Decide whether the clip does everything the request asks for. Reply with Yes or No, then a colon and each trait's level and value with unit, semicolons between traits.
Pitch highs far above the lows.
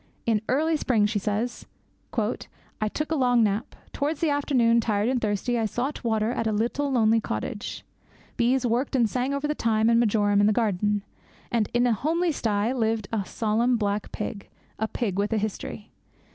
No: average, 3.1 semitones